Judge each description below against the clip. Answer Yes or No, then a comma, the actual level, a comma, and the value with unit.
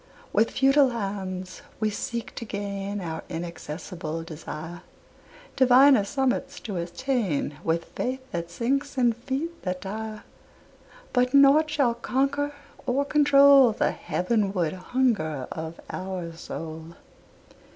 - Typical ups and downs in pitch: No, wide, 7.4 semitones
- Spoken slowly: Yes, slow, 115 wpm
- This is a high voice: Yes, high, 215 Hz